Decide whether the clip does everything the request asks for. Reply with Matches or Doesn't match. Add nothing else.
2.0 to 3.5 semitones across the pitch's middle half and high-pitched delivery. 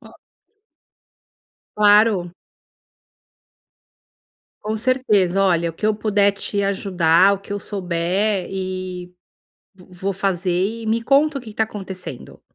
Matches